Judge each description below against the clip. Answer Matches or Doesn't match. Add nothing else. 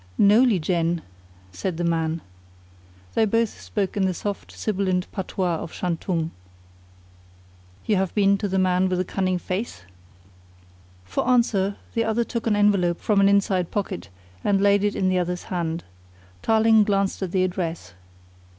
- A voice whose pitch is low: Doesn't match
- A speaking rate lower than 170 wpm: Matches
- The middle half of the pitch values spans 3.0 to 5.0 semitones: Doesn't match